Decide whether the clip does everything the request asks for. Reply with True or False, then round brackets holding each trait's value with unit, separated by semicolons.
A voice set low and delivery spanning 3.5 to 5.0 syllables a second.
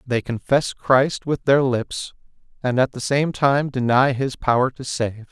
True (130 Hz; 4.0 syllables/s)